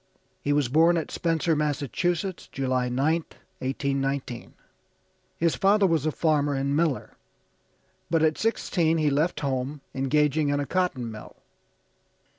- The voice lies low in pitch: No, medium, 150 Hz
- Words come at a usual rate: No, slow, 130 wpm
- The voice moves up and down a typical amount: Yes, average, 3.3 semitones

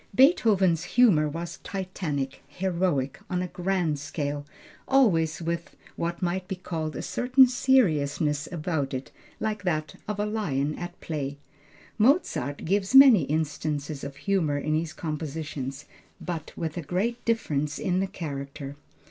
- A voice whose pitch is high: No, medium, 165 Hz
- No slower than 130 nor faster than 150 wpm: Yes, average, 140 wpm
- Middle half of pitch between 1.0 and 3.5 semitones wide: No, average, 4.7 semitones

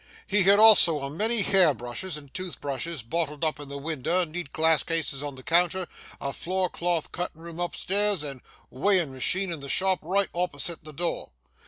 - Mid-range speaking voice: Yes, medium, 165 Hz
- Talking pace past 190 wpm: Yes, average, 200 wpm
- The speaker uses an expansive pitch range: No, average, 4.3 semitones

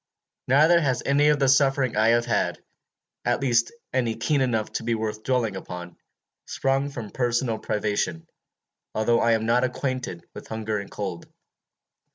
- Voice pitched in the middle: No, low, 120 Hz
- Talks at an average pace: Yes, average, 160 wpm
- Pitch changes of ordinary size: Yes, average, 3.5 semitones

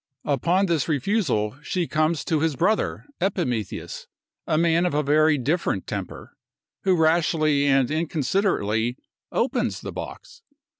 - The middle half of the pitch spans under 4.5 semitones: Yes, average, 3.8 semitones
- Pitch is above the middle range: No, medium, 155 Hz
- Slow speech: Yes, slow, 130 wpm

